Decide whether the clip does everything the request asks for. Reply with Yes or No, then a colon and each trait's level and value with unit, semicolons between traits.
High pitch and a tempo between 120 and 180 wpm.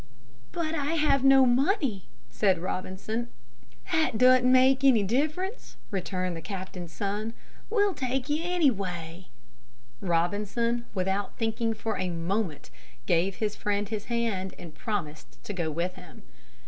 Yes: high, 210 Hz; slow, 135 wpm